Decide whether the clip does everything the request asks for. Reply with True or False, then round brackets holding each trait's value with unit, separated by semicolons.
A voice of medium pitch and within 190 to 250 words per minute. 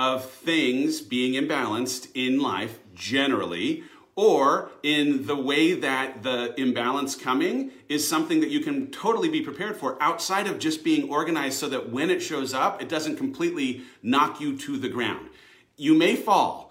False (155 Hz; 165 wpm)